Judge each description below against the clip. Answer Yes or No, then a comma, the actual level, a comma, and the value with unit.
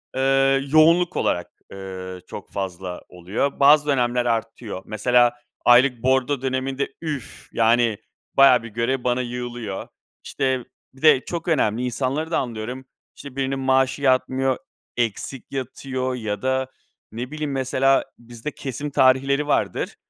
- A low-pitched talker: Yes, low, 130 Hz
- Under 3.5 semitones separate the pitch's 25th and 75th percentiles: Yes, narrow, 2.5 semitones